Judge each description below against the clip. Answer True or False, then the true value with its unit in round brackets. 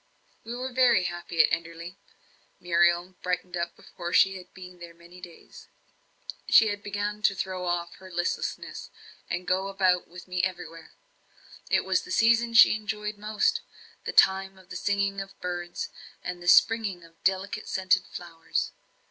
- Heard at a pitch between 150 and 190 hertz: True (185 Hz)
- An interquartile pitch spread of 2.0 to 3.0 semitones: True (2.7 semitones)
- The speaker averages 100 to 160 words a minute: True (155 wpm)